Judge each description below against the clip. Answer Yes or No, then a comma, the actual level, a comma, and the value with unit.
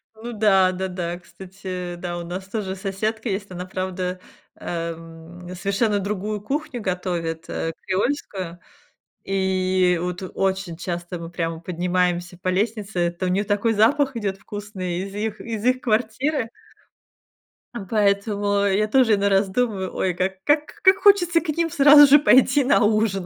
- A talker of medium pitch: No, high, 195 Hz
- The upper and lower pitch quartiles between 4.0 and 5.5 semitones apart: No, average, 3.3 semitones